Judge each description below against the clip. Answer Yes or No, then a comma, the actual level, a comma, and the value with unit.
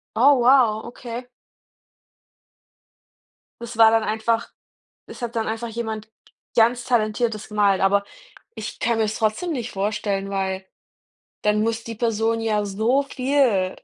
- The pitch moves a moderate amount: No, narrow, 2.1 semitones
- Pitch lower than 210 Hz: No, high, 225 Hz